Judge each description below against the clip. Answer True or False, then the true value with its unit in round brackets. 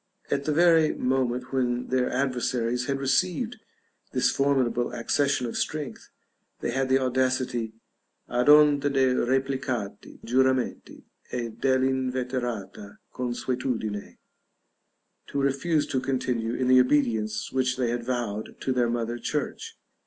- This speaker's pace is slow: True (125 wpm)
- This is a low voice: True (130 Hz)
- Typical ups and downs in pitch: False (2.1 semitones)